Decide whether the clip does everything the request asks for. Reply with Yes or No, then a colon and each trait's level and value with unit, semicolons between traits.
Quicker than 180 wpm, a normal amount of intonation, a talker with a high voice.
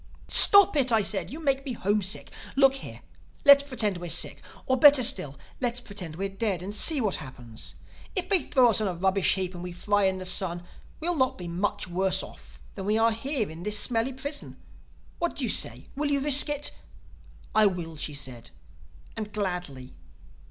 No: average, 190 wpm; wide, 7.0 semitones; high, 205 Hz